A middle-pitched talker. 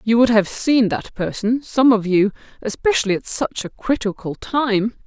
No: high, 225 Hz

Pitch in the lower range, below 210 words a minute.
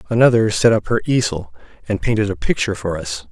Yes: low, 105 Hz; average, 200 wpm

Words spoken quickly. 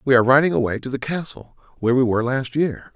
Yes: fast, 245 wpm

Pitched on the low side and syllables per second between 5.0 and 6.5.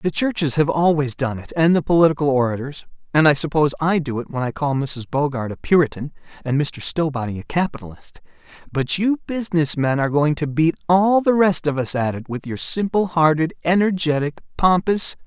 No: medium, 155 Hz; 5.5 syllables/s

